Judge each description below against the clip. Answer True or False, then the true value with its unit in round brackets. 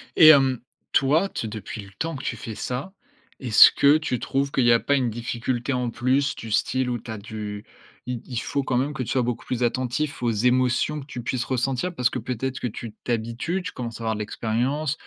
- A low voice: True (125 Hz)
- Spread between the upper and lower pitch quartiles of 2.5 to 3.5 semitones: True (2.8 semitones)